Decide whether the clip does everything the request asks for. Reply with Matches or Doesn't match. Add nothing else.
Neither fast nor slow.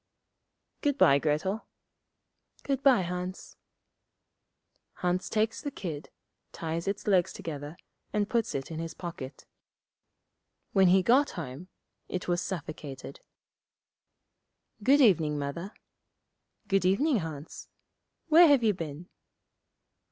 Doesn't match